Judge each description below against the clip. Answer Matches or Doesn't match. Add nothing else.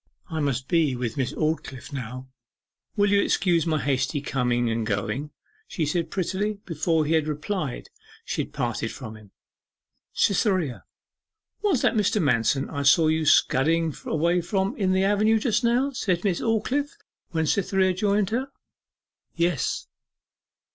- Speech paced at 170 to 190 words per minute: Doesn't match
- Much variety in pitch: Matches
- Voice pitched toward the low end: Doesn't match